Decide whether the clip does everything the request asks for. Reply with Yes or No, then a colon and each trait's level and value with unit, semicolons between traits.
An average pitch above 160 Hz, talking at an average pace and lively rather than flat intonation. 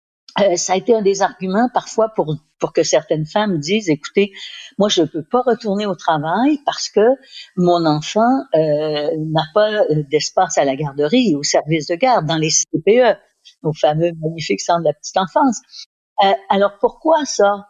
Yes: medium, 185 Hz; average, 180 wpm; wide, 6.1 semitones